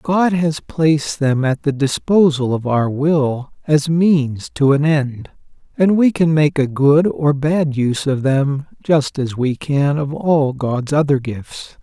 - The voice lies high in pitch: No, medium, 145 Hz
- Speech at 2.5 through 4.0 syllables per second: Yes, 3.6 syllables/s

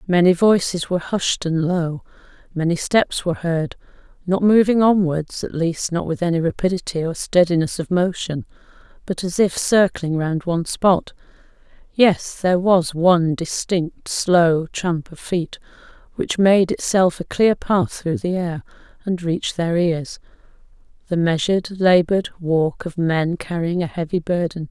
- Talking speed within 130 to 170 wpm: Yes, average, 150 wpm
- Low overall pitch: No, medium, 175 Hz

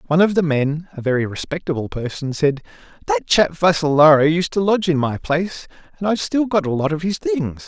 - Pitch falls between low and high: Yes, medium, 160 Hz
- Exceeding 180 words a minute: Yes, average, 195 wpm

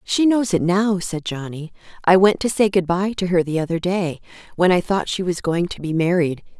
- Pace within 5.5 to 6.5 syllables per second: No, 5.1 syllables/s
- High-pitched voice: No, medium, 180 Hz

